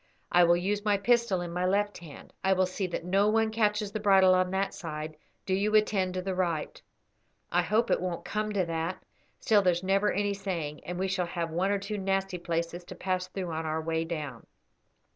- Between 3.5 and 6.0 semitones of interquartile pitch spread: No, average, 2.8 semitones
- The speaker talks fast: Yes, fast, 220 wpm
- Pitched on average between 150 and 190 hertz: Yes, medium, 185 Hz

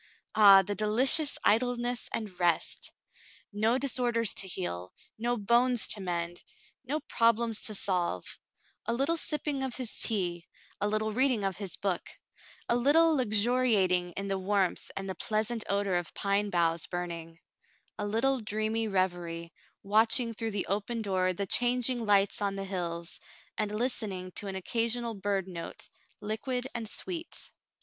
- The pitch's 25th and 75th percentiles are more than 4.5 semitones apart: No, average, 4.1 semitones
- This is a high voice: Yes, high, 210 Hz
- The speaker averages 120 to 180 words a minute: Yes, average, 160 wpm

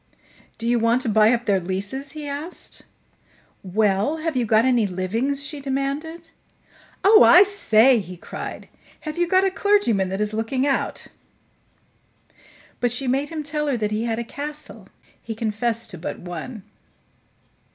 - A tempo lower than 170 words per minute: Yes, average, 160 wpm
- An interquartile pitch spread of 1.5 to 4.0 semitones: No, wide, 5.5 semitones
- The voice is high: Yes, high, 245 Hz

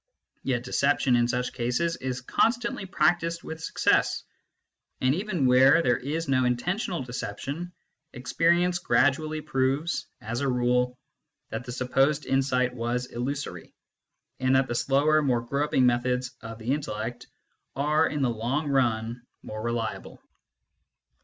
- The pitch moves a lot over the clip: No, average, 3.7 semitones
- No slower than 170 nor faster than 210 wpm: No, slow, 135 wpm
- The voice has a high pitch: No, low, 130 Hz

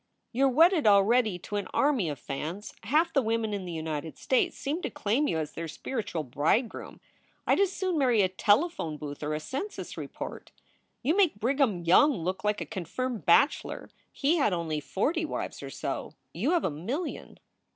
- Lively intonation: Yes, wide, 9.0 semitones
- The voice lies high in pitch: Yes, high, 215 Hz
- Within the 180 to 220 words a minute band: Yes, average, 190 wpm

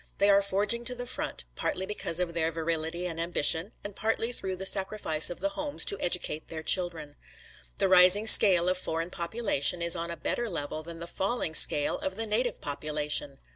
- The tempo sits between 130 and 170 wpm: No, average, 195 wpm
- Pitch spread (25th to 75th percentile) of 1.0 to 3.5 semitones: No, average, 3.9 semitones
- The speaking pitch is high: No, medium, 180 Hz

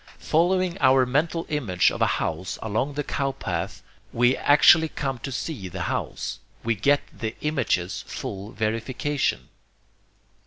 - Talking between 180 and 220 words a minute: No, average, 140 wpm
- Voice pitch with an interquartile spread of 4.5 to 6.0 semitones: Yes, average, 5.0 semitones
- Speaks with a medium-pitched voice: No, low, 130 Hz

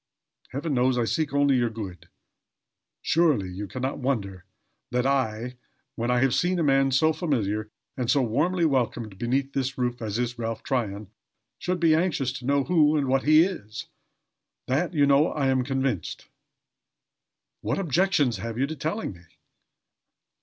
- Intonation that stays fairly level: No, average, 4.3 semitones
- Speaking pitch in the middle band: No, low, 130 Hz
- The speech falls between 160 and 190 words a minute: Yes, average, 165 wpm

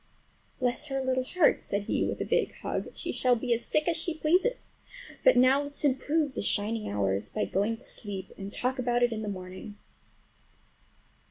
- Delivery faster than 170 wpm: Yes, average, 190 wpm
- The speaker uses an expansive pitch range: Yes, wide, 5.8 semitones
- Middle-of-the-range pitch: No, high, 245 Hz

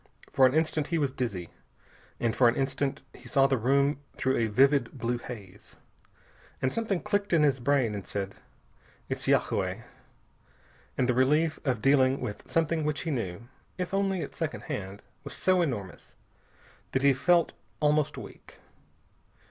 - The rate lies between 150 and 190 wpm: Yes, average, 160 wpm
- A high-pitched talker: No, low, 135 Hz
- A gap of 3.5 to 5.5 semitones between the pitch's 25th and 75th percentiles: Yes, average, 4.3 semitones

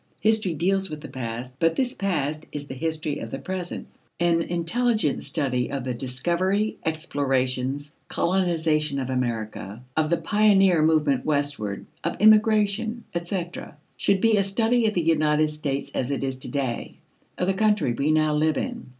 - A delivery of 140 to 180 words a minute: Yes, average, 165 wpm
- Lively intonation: Yes, wide, 5.8 semitones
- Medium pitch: Yes, medium, 155 Hz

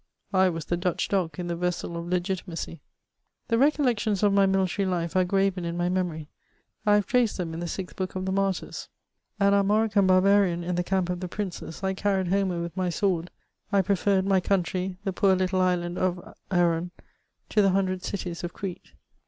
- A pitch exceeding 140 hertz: Yes, medium, 185 Hz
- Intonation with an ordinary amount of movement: No, narrow, 2.0 semitones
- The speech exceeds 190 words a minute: Yes, average, 200 wpm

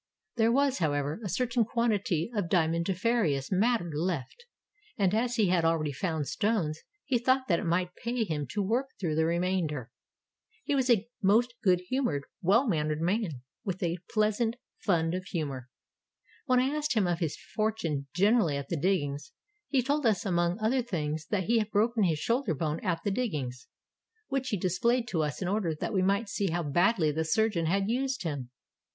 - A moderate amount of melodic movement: No, wide, 6.2 semitones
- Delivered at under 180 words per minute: No, average, 185 wpm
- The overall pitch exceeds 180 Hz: Yes, high, 190 Hz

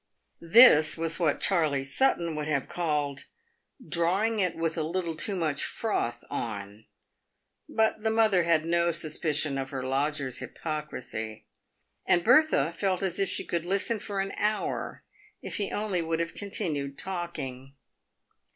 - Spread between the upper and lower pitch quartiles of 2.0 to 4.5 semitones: No, average, 5.0 semitones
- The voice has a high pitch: No, medium, 165 Hz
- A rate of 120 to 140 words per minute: No, average, 160 wpm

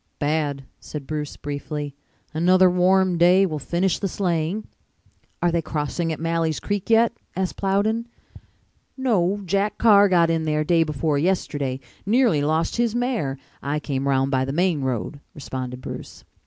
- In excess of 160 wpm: No, average, 155 wpm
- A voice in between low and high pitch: Yes, medium, 165 Hz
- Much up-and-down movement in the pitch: No, average, 4.6 semitones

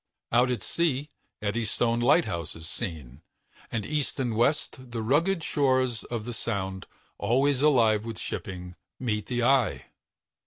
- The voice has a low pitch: Yes, low, 120 Hz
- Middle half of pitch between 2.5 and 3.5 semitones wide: No, average, 3.9 semitones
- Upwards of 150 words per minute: No, average, 145 wpm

